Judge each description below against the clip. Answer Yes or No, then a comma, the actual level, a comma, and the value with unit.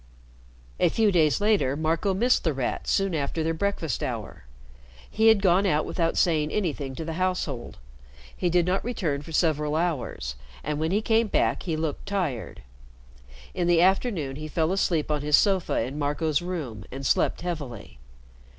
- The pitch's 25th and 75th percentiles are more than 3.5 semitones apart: Yes, average, 4.1 semitones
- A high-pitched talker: No, medium, 165 Hz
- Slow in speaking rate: No, average, 170 wpm